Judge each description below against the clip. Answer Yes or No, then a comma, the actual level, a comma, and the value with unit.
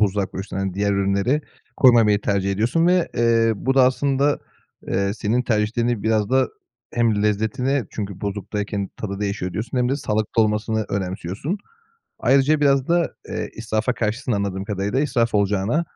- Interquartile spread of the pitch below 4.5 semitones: Yes, average, 4.0 semitones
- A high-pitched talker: No, low, 110 Hz